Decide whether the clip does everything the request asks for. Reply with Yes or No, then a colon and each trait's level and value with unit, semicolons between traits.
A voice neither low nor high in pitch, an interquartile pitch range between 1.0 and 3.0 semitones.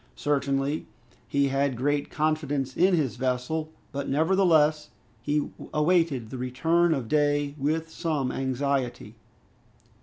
Yes: medium, 145 Hz; average, 2.7 semitones